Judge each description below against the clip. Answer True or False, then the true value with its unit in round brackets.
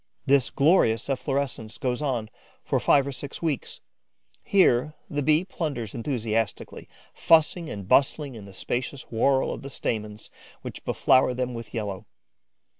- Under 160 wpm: True (140 wpm)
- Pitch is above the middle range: False (130 Hz)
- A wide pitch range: False (4.2 semitones)